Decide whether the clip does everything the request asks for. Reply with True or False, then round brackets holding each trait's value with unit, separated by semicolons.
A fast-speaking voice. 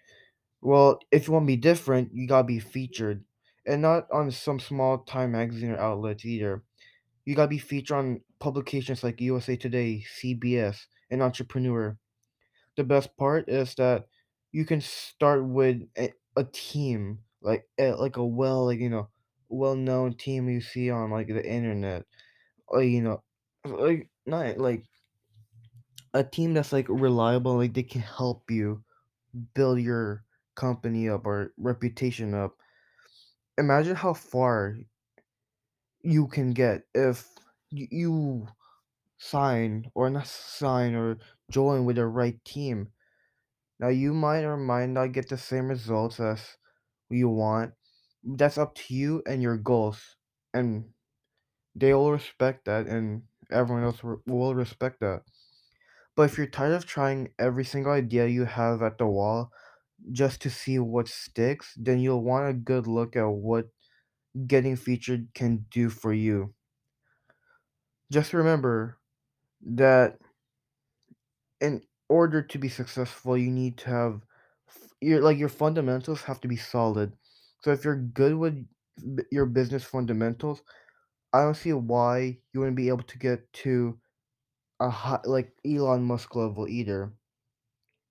False (145 wpm)